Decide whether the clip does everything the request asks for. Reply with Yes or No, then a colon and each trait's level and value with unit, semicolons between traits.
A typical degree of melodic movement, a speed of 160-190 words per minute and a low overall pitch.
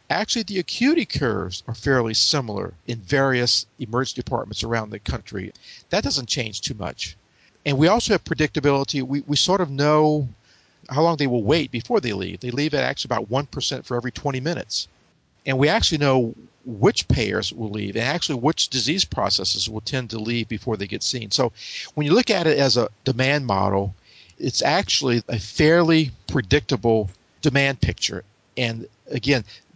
Yes: average, 4.9 semitones; average, 175 wpm; low, 130 Hz